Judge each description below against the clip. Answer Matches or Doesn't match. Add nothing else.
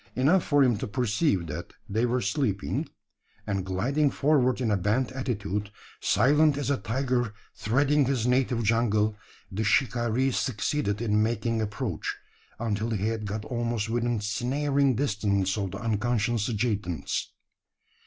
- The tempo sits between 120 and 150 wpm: Matches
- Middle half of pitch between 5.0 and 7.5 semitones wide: Doesn't match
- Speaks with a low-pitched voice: Matches